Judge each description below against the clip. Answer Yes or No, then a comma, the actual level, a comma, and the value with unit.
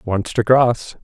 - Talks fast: No, average, 175 wpm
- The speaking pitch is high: No, low, 115 Hz